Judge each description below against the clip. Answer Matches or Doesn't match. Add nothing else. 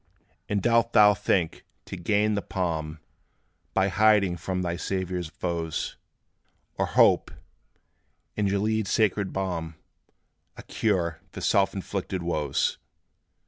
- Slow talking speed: Matches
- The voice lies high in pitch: Doesn't match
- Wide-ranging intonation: Doesn't match